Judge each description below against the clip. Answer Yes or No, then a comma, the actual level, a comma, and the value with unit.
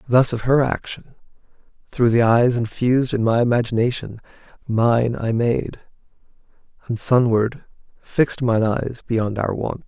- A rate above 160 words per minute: No, slow, 135 wpm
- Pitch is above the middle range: No, low, 120 Hz